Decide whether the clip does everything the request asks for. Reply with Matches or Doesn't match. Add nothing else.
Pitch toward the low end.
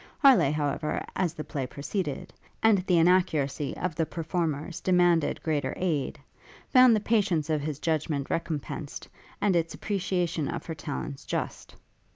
Doesn't match